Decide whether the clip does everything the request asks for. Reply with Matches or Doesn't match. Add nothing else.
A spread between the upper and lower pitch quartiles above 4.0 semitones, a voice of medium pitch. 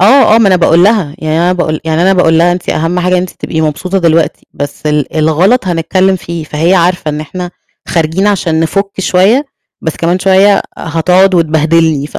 Doesn't match